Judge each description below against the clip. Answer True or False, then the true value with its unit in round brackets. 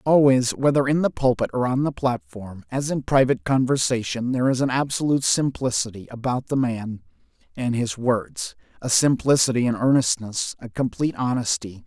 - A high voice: False (130 Hz)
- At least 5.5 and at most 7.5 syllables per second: False (5.3 syllables/s)